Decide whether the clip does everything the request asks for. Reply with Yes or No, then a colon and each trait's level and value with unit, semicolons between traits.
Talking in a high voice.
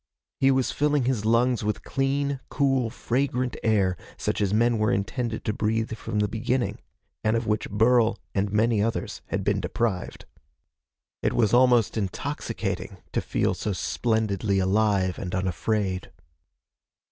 No: low, 110 Hz